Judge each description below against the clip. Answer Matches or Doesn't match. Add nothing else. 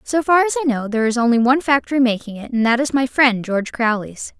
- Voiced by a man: Doesn't match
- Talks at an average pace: Doesn't match